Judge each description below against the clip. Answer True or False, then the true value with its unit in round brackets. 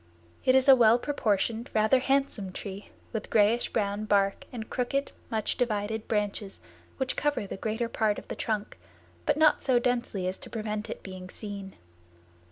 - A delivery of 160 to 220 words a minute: True (170 wpm)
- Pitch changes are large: False (3.3 semitones)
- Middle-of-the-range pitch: False (220 Hz)